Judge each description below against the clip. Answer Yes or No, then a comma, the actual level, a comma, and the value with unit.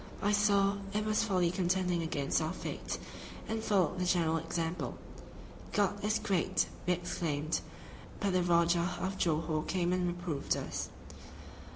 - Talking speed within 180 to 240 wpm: No, average, 145 wpm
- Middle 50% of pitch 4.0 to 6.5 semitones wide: No, average, 2.8 semitones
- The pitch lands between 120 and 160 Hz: No, medium, 180 Hz